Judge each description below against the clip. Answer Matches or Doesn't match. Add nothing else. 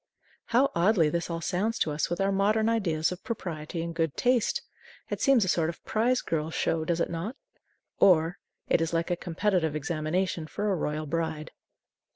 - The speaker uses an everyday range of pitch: Matches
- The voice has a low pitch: Doesn't match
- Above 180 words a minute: Matches